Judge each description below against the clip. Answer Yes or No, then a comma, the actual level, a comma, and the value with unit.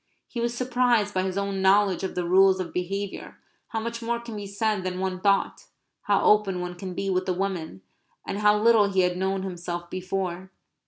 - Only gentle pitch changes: Yes, narrow, 2.3 semitones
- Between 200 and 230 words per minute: Yes, fast, 205 wpm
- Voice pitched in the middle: No, high, 195 Hz